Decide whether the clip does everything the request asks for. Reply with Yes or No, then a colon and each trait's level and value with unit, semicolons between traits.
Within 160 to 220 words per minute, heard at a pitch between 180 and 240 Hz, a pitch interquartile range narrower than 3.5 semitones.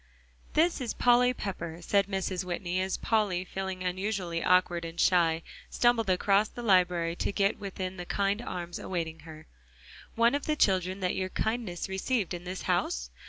Yes: average, 165 wpm; medium, 185 Hz; average, 2.8 semitones